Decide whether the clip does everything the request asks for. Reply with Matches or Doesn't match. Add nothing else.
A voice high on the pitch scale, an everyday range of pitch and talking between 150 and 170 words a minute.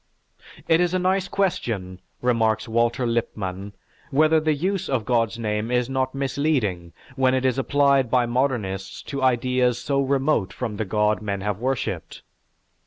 Doesn't match